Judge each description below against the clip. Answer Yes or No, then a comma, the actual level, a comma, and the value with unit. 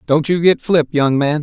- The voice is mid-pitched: Yes, medium, 155 Hz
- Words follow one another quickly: Yes, fast, 255 wpm